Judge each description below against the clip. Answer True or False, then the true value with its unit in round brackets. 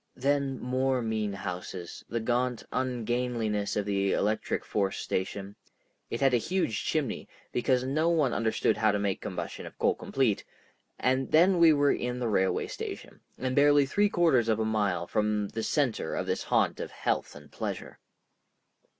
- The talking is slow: False (160 wpm)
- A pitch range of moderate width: True (4.2 semitones)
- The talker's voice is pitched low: True (120 Hz)